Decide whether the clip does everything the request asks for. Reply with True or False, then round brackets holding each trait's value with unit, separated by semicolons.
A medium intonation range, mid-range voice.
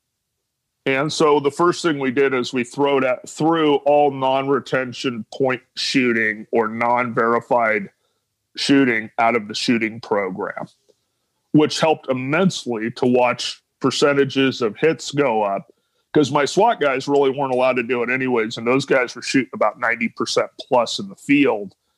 False (3.2 semitones; 130 Hz)